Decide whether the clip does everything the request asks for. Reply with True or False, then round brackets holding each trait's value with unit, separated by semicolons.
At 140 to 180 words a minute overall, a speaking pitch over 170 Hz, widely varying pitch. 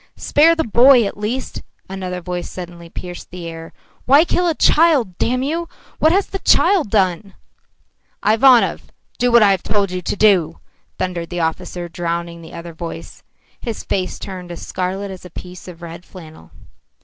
True (170 wpm; 185 Hz; 5.7 semitones)